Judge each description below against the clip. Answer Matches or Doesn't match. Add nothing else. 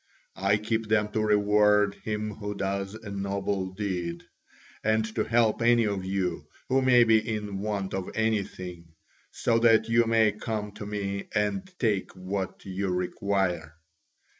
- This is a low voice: Matches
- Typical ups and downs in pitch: Doesn't match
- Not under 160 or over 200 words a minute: Doesn't match